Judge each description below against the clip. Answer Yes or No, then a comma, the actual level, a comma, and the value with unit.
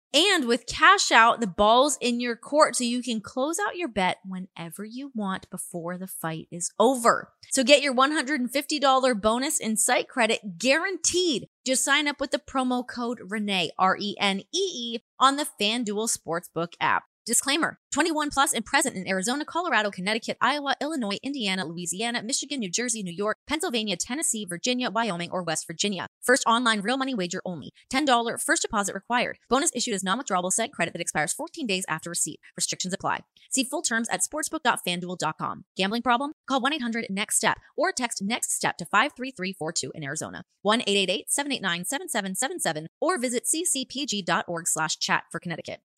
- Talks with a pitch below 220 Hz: No, high, 230 Hz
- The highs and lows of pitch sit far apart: Yes, wide, 6.3 semitones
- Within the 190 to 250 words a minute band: No, average, 165 wpm